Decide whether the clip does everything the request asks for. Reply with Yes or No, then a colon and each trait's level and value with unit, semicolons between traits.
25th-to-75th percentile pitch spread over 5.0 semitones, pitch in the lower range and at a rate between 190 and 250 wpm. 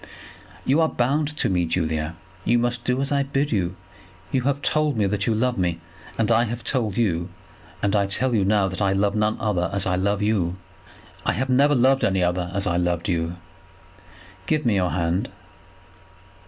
Yes: wide, 5.5 semitones; low, 105 Hz; average, 195 wpm